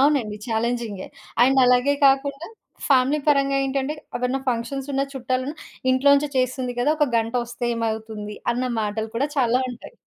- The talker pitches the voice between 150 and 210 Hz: No, very high, 255 Hz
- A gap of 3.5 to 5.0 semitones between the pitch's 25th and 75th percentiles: No, average, 2.9 semitones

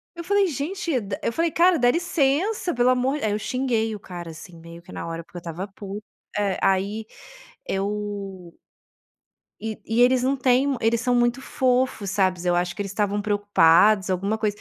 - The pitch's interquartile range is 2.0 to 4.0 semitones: No, average, 5.0 semitones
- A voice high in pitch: Yes, high, 215 Hz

